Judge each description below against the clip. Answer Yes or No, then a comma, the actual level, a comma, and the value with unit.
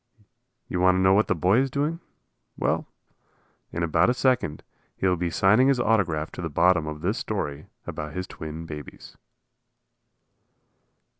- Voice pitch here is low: Yes, very low, 90 Hz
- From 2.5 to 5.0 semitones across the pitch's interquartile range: No, wide, 5.4 semitones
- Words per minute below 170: Yes, average, 160 wpm